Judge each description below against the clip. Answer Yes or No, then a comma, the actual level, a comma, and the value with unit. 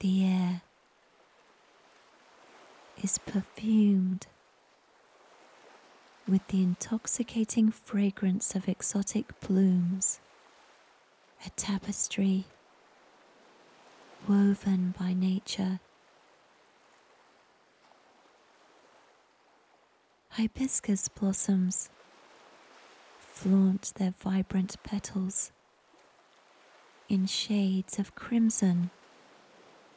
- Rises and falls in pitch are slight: Yes, narrow, 1.5 semitones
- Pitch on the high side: Yes, high, 195 Hz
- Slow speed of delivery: Yes, slow, 50 wpm